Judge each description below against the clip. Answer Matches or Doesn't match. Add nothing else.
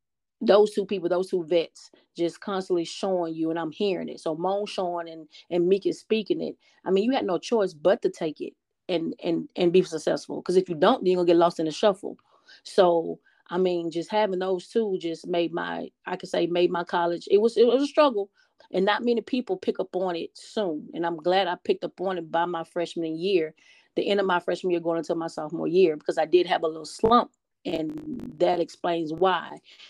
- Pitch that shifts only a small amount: Doesn't match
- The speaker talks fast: Matches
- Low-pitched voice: Doesn't match